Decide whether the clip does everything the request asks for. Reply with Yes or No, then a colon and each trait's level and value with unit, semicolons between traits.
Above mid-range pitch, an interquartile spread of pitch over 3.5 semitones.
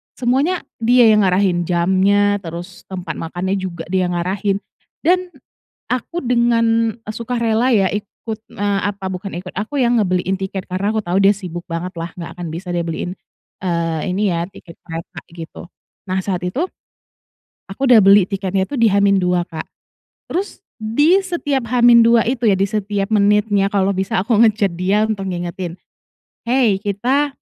Yes: high, 200 Hz; average, 4.0 semitones